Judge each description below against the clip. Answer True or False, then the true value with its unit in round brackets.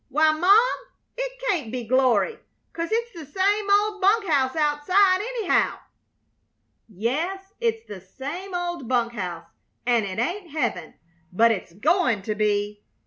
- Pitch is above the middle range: True (310 Hz)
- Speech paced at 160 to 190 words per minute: False (140 wpm)